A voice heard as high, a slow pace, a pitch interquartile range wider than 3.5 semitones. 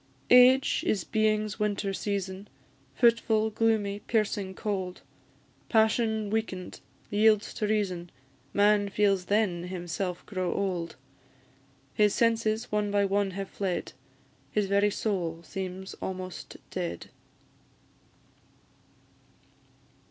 No: high, 205 Hz; slow, 100 wpm; narrow, 2.4 semitones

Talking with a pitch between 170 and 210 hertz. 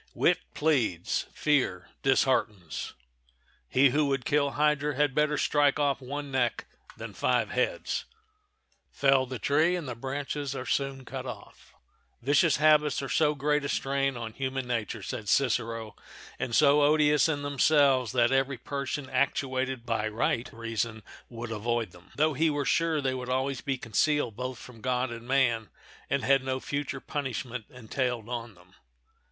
No: low, 135 Hz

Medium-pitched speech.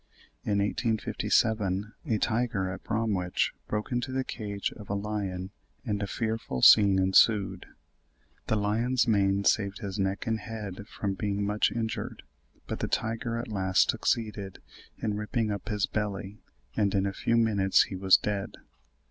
No: low, 105 Hz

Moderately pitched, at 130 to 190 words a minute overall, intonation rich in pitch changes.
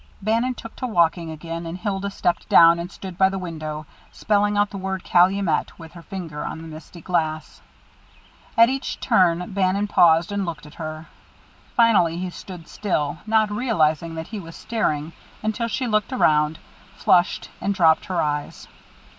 No: medium, 180 Hz; average, 170 wpm; average, 4.0 semitones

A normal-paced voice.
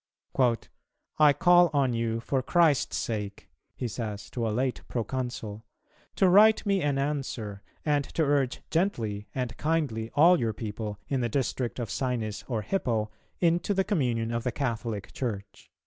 Yes: average, 165 wpm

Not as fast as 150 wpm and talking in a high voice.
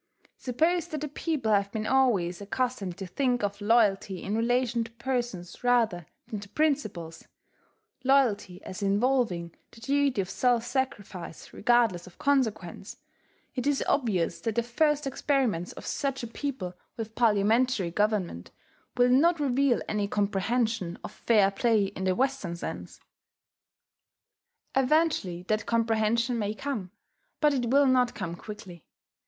Yes: average, 140 wpm; high, 230 Hz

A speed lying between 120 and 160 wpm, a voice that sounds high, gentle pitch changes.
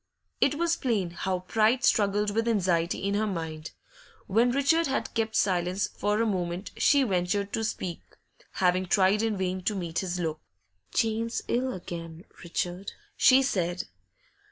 No: average, 155 wpm; high, 200 Hz; average, 4.1 semitones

